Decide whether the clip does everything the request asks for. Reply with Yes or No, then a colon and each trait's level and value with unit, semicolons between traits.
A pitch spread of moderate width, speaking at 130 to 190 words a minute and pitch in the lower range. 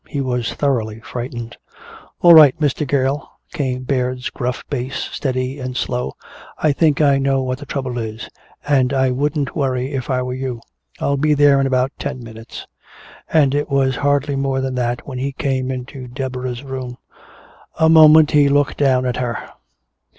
No: narrow, 2.0 semitones; average, 170 wpm; low, 130 Hz